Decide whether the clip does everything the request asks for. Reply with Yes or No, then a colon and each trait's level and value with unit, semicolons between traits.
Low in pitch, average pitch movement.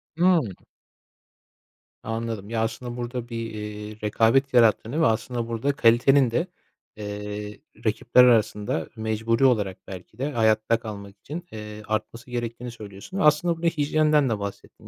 Yes: low, 115 Hz; average, 3.2 semitones